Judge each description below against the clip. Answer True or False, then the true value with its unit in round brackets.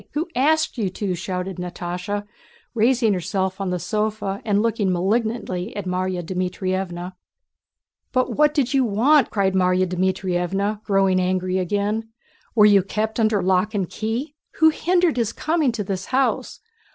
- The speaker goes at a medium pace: True (150 wpm)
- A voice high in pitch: True (200 Hz)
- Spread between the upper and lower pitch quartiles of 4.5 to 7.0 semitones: False (3.7 semitones)